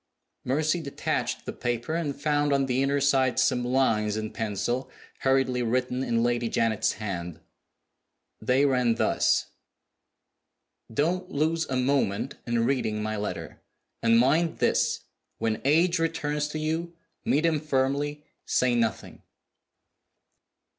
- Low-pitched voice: Yes, low, 130 Hz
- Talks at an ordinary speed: No, slow, 125 wpm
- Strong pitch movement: No, average, 4.2 semitones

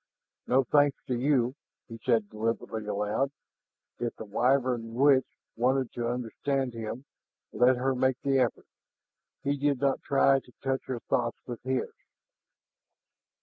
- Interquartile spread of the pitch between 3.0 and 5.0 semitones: No, narrow, 2.4 semitones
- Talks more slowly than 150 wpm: Yes, average, 140 wpm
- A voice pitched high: No, low, 125 Hz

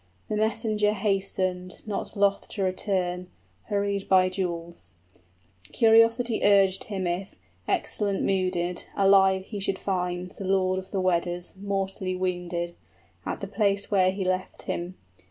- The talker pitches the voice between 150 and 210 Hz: Yes, high, 190 Hz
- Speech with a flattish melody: Yes, narrow, 1.6 semitones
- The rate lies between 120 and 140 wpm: Yes, slow, 135 wpm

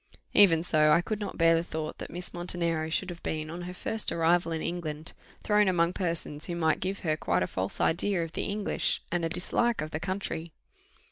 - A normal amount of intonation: No, narrow, 2.3 semitones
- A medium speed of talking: No, fast, 215 wpm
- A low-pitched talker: No, medium, 170 Hz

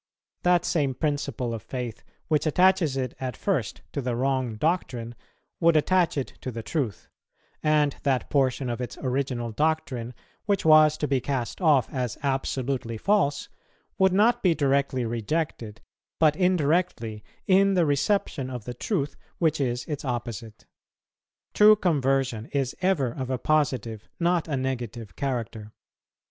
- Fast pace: No, average, 145 wpm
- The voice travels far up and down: No, average, 4.5 semitones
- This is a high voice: No, low, 135 Hz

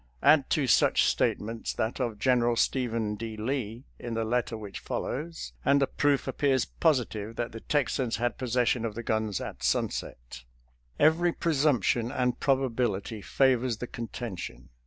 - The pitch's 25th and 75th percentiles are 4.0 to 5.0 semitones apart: No, average, 3.2 semitones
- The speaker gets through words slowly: No, average, 150 wpm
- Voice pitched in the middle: No, low, 120 Hz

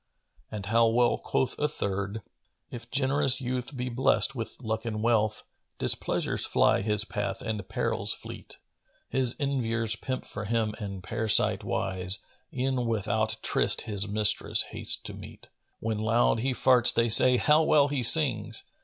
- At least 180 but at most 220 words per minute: No, average, 160 wpm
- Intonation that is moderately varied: Yes, average, 3.1 semitones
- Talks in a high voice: No, low, 115 Hz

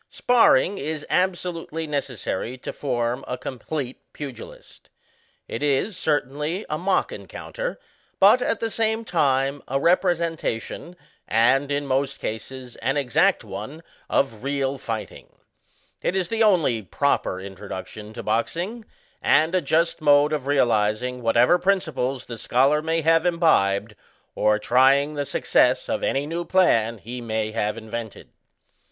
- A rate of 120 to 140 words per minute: Yes, slow, 135 wpm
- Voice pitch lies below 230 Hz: Yes, medium, 140 Hz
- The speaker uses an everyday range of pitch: No, wide, 5.9 semitones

